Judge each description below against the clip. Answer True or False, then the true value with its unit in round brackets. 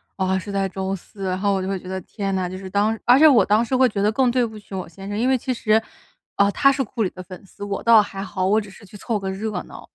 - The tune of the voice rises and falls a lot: False (2.8 semitones)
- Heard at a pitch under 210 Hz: True (200 Hz)